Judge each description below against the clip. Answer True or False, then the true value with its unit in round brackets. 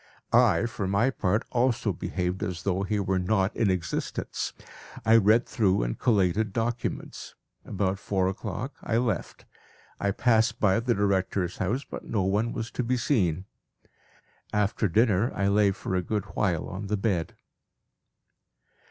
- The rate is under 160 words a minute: True (150 wpm)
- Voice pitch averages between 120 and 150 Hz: False (100 Hz)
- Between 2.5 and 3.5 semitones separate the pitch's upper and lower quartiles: True (3.2 semitones)